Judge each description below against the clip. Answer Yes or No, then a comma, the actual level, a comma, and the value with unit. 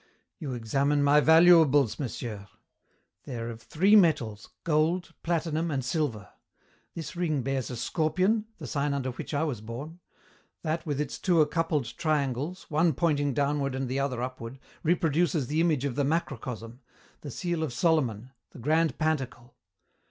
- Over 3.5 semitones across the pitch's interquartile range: Yes, average, 4.2 semitones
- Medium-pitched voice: Yes, medium, 145 Hz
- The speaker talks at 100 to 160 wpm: Yes, average, 155 wpm